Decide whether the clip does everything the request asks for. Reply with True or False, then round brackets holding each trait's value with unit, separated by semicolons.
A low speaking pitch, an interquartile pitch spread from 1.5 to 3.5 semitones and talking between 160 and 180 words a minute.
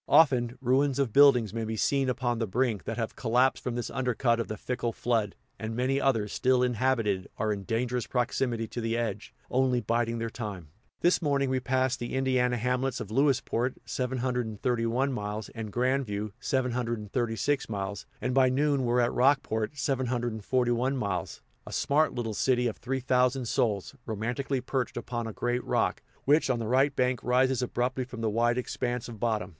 True (125 Hz; 2.4 semitones; 175 wpm)